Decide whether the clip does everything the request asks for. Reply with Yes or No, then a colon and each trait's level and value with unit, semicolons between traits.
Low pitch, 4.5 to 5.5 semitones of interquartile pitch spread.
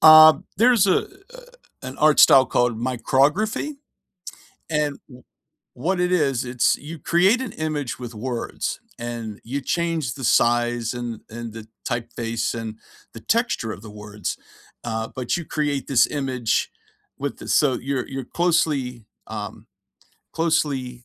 Yes: low, 130 Hz; average, 5.0 semitones